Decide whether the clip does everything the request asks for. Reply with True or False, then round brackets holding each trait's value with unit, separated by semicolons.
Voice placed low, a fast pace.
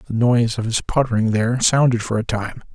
True (115 Hz; 220 wpm)